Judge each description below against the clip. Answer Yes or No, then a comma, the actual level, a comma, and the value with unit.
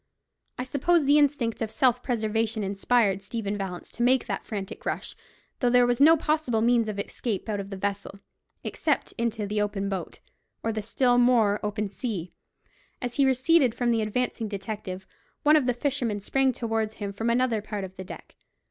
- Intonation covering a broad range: No, average, 3.5 semitones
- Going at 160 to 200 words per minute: Yes, average, 185 wpm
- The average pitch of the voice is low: No, high, 225 Hz